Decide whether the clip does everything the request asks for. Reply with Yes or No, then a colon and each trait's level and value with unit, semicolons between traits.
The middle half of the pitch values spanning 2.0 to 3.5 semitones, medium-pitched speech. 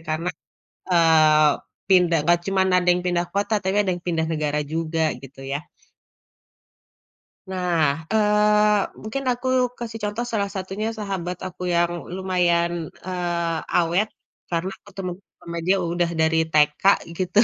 Yes: average, 3.2 semitones; medium, 180 Hz